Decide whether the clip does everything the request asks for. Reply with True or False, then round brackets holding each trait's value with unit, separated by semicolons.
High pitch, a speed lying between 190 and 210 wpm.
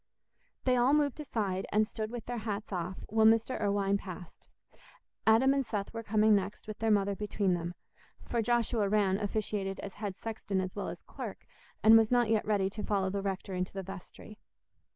True (210 Hz; 195 wpm)